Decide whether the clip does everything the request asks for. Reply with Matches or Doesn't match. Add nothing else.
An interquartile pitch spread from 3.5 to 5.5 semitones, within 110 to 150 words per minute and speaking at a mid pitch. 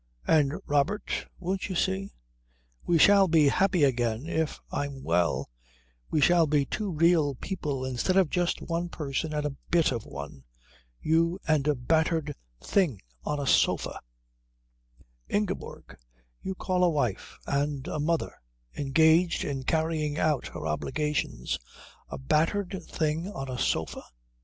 Matches